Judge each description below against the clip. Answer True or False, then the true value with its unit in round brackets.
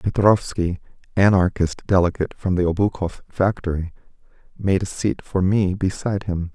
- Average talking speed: False (130 wpm)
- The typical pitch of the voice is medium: False (95 Hz)